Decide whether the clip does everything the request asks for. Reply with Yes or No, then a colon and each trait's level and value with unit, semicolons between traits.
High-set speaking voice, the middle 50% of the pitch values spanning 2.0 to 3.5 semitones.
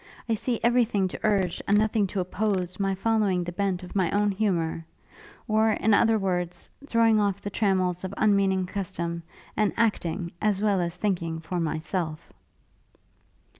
Yes: high, 195 Hz; average, 3.1 semitones